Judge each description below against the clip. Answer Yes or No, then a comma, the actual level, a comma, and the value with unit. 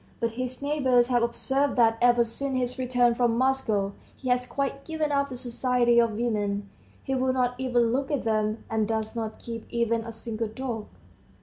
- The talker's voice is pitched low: No, high, 240 Hz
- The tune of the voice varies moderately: No, narrow, 2.3 semitones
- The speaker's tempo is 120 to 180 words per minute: No, average, 190 wpm